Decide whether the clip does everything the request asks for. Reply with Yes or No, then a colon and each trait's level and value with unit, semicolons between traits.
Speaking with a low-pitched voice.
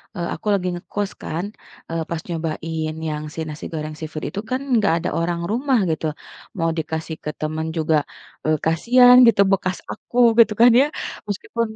No: medium, 165 Hz